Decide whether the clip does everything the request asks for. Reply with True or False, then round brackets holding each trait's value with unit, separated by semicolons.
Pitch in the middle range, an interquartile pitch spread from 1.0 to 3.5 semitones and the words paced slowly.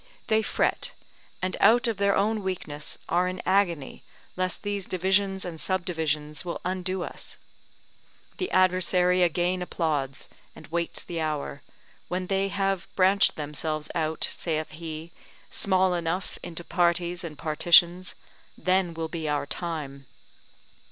True (175 Hz; 2.8 semitones; 130 wpm)